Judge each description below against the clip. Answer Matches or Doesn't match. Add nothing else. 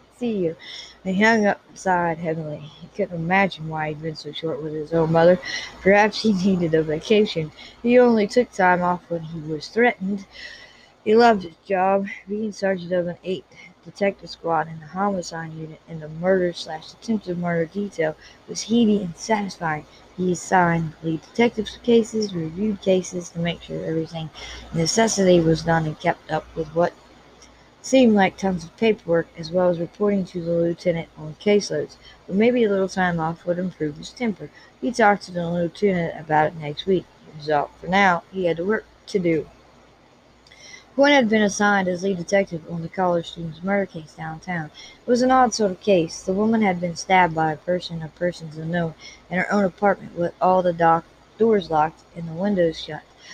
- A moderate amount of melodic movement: Matches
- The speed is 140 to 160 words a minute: Doesn't match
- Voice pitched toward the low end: Doesn't match